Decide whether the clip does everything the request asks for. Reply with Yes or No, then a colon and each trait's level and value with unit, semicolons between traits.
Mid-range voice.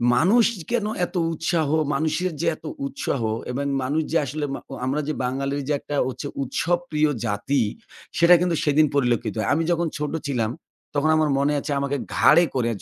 Yes: medium, 150 Hz